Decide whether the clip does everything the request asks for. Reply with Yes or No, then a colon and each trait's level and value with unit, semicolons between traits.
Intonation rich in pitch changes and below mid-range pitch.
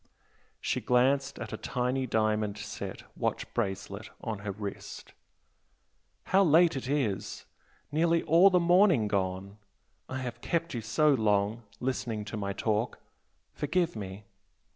Yes: wide, 6.0 semitones; low, 120 Hz